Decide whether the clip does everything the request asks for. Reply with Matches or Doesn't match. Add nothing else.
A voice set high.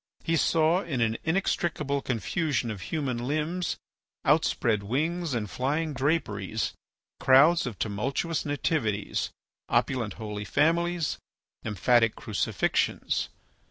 Doesn't match